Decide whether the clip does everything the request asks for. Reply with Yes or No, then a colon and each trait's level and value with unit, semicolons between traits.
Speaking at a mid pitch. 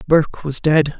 Yes: medium, 150 Hz